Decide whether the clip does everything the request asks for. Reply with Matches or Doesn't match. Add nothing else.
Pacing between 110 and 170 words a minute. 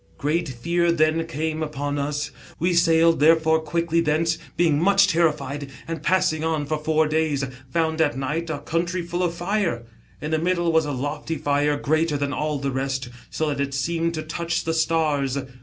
Doesn't match